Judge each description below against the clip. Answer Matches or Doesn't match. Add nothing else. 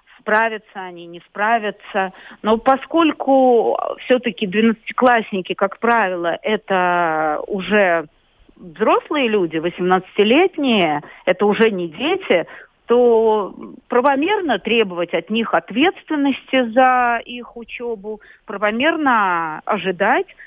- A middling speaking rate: Doesn't match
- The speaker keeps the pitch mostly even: Doesn't match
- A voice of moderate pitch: Doesn't match